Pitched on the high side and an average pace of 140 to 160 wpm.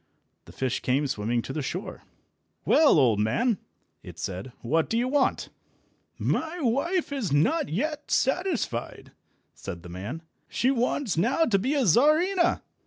Yes: high, 230 Hz; average, 150 wpm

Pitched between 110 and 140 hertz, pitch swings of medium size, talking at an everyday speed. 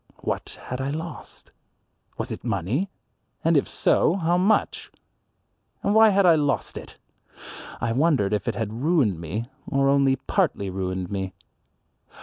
No: low, 135 Hz; wide, 8.5 semitones; average, 145 wpm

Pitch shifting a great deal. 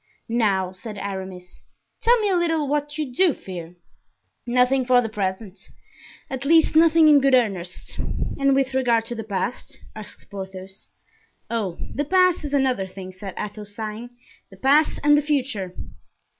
Yes: wide, 6.8 semitones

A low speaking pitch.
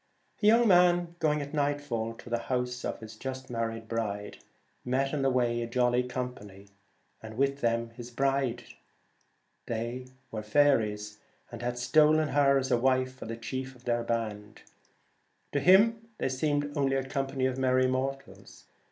Yes: low, 130 Hz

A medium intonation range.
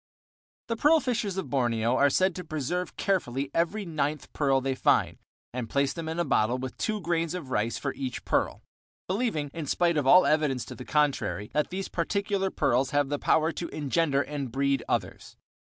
Yes: average, 4.9 semitones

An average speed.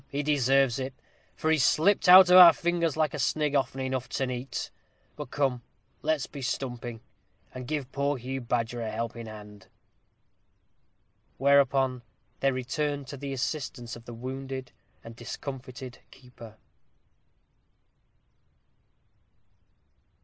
No: slow, 125 wpm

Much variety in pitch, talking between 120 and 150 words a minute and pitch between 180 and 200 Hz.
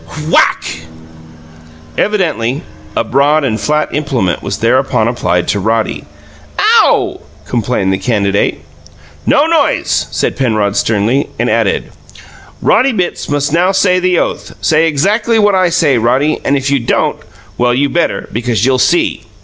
No: wide, 7.0 semitones; average, 140 wpm; low, 135 Hz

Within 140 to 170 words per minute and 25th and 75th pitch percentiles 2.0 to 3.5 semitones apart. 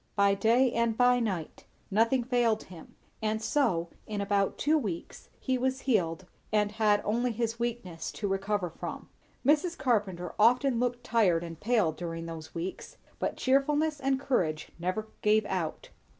No: average, 155 wpm; average, 5.0 semitones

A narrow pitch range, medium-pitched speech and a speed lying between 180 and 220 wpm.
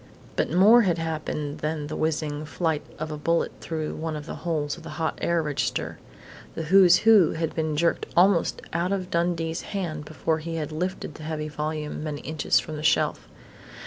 Yes: narrow, 2.0 semitones; medium, 160 Hz; average, 190 wpm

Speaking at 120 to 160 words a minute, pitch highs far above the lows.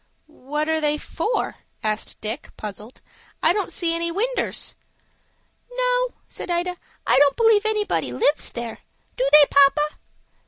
Yes: slow, 135 wpm; wide, 7.2 semitones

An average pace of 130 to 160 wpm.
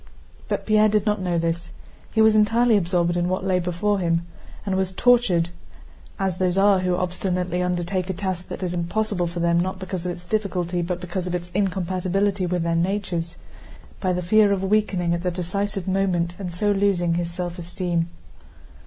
No: average, 180 wpm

